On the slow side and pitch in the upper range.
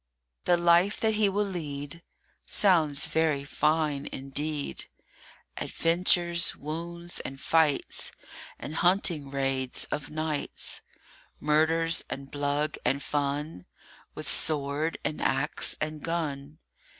No: slow, 105 wpm; medium, 155 Hz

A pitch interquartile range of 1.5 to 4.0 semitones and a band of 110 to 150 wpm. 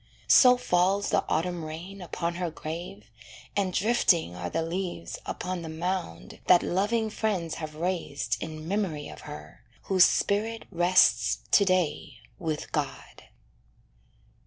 Yes: average, 3.6 semitones; slow, 135 wpm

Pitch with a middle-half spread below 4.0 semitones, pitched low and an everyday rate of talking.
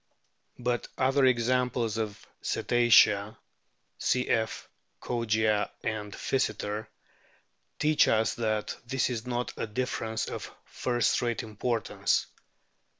No: narrow, 2.4 semitones; low, 115 Hz; slow, 100 wpm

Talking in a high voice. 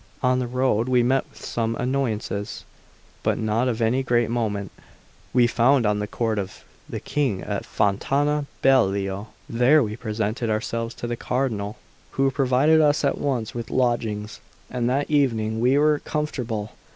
No: low, 120 Hz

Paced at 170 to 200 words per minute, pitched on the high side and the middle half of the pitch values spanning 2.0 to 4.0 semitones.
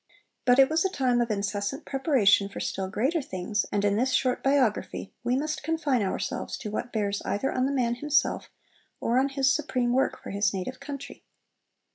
No: average, 190 wpm; very high, 250 Hz; average, 5.0 semitones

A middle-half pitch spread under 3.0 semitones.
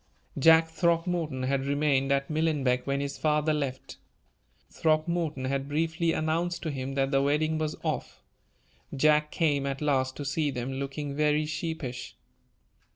Yes: narrow, 2.5 semitones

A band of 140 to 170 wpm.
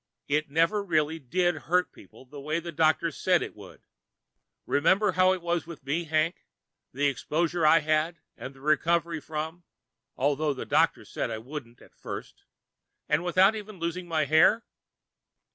Yes: average, 160 wpm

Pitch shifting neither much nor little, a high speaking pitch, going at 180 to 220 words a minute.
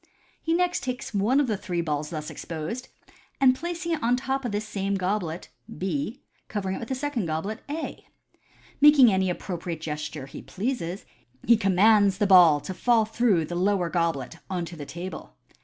No: wide, 6.4 semitones; high, 195 Hz; average, 190 wpm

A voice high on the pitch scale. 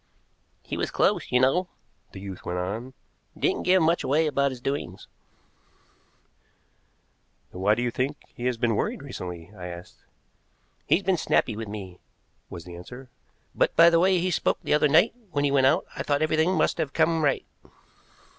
No: low, 135 Hz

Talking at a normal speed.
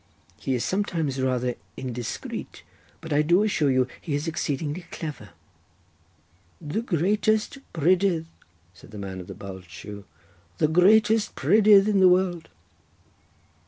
No: slow, 130 wpm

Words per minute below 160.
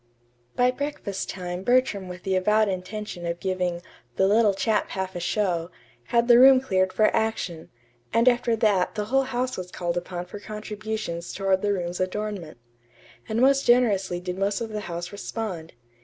No: average, 170 wpm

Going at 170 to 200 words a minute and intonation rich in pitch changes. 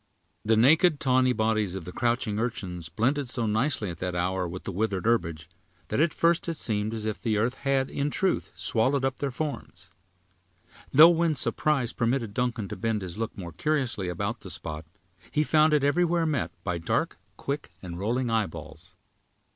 Yes: average, 180 wpm; wide, 6.4 semitones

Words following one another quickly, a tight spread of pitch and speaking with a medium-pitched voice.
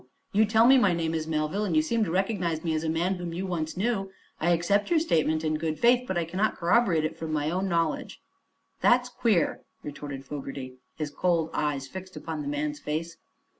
No: fast, 210 wpm; average, 3.8 semitones; medium, 170 Hz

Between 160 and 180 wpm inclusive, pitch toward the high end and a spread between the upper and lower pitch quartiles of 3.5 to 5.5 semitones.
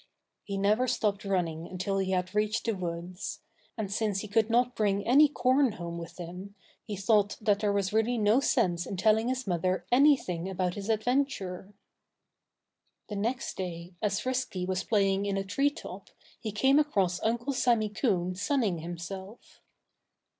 Yes: average, 165 wpm; high, 205 Hz; average, 3.9 semitones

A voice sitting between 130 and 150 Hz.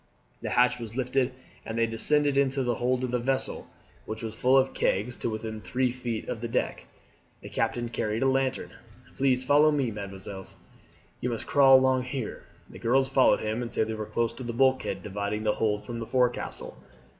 No: low, 120 Hz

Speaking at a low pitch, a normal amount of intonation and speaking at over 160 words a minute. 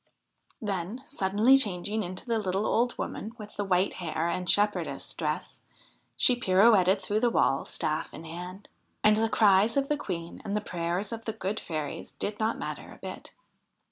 No: high, 200 Hz; average, 3.5 semitones; average, 175 wpm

